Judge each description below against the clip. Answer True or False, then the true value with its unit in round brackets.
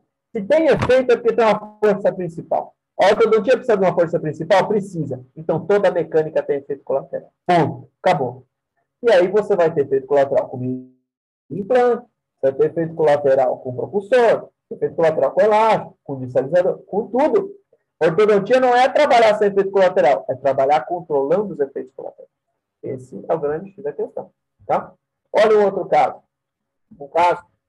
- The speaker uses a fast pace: False (170 wpm)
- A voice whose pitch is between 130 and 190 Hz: False (200 Hz)